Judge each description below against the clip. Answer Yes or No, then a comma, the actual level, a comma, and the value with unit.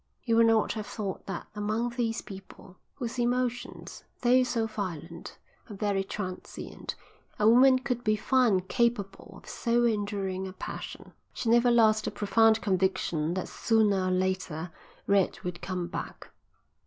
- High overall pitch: Yes, high, 210 Hz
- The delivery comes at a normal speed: Yes, average, 150 wpm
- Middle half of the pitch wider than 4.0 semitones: No, average, 3.7 semitones